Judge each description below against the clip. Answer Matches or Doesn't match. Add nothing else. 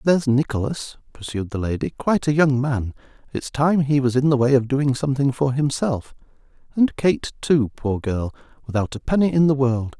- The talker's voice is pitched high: Doesn't match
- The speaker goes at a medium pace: Matches